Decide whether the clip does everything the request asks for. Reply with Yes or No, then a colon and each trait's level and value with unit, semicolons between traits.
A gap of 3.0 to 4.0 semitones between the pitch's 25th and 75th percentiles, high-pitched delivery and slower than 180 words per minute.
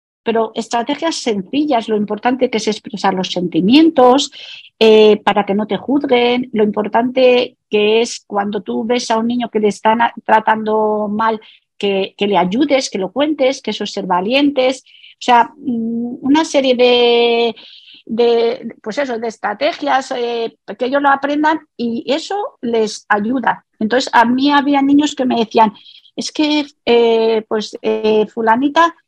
Yes: average, 3.6 semitones; high, 235 Hz; average, 160 wpm